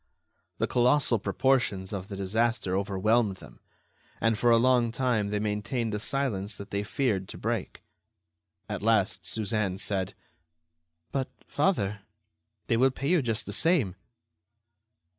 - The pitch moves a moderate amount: Yes, average, 3.8 semitones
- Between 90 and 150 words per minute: Yes, average, 140 wpm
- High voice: No, low, 110 Hz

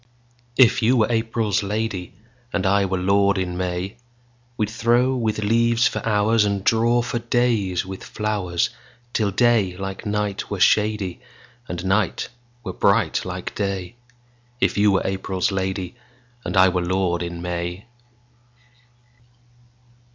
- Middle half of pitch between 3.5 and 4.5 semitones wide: Yes, average, 3.8 semitones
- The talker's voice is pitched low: Yes, low, 105 Hz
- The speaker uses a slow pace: Yes, slow, 115 wpm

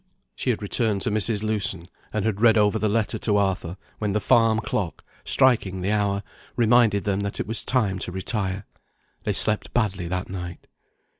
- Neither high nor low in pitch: No, low, 105 Hz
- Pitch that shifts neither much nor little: No, narrow, 2.3 semitones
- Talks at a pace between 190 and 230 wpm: No, average, 180 wpm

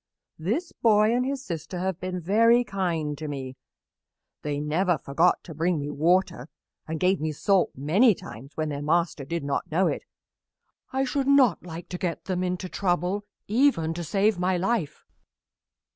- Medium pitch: Yes, medium, 180 Hz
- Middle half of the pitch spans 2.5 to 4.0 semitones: No, average, 4.4 semitones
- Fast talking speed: No, average, 170 wpm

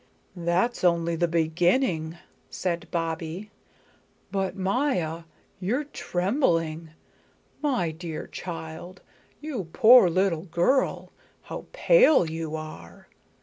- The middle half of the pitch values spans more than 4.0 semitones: No, average, 3.6 semitones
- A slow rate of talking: Yes, slow, 95 wpm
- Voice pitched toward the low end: No, medium, 175 Hz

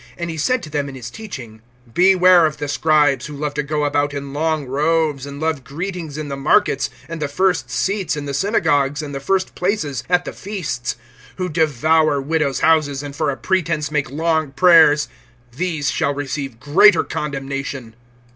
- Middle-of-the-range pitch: Yes, medium, 150 Hz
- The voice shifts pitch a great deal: No, average, 3.0 semitones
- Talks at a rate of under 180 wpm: No, average, 185 wpm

